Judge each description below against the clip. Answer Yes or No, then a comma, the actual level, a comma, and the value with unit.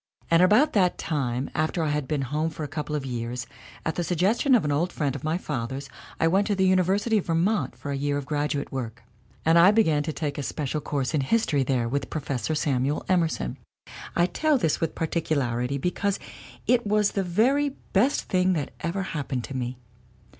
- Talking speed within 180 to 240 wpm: Yes, fast, 205 wpm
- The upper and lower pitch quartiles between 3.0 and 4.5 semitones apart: No, average, 5.0 semitones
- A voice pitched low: No, medium, 155 Hz